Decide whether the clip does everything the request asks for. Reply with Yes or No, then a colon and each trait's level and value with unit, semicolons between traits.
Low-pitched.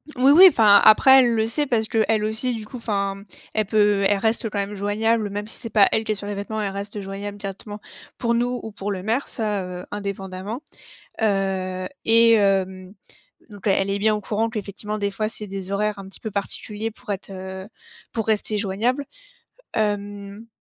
No: high, 205 Hz